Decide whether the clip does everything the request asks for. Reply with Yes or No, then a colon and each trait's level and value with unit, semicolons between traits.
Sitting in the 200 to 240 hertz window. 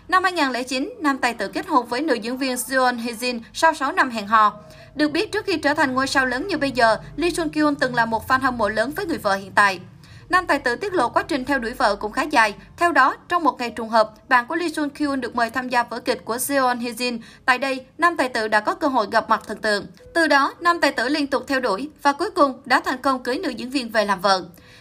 No: very high, 260 Hz